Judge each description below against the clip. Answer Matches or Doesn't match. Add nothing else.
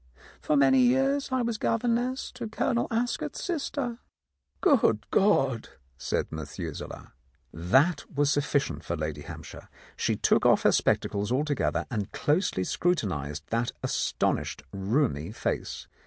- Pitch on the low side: Doesn't match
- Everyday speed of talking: Doesn't match